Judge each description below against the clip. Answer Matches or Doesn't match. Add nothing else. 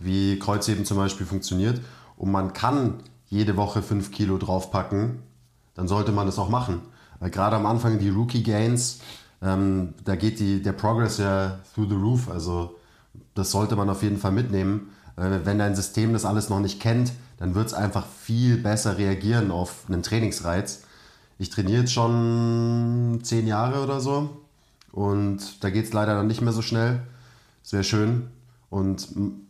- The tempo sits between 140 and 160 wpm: Doesn't match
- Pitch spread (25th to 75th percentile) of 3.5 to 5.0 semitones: Doesn't match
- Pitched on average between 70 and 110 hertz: Matches